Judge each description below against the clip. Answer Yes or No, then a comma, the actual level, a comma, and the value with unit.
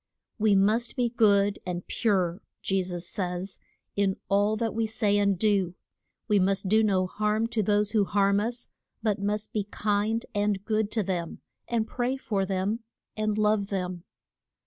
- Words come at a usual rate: Yes, average, 170 wpm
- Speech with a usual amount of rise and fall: No, narrow, 2.0 semitones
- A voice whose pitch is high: Yes, high, 205 Hz